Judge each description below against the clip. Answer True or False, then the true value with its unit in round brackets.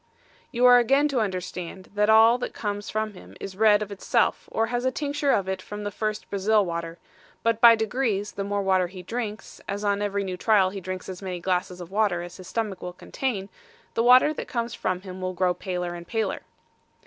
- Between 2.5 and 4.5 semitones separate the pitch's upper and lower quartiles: True (3.3 semitones)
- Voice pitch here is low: False (205 Hz)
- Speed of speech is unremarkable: False (220 wpm)